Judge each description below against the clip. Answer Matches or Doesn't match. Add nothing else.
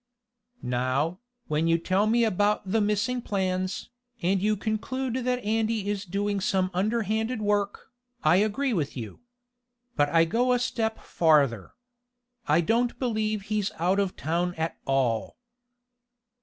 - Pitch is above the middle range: Matches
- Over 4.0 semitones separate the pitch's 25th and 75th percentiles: Matches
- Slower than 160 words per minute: Matches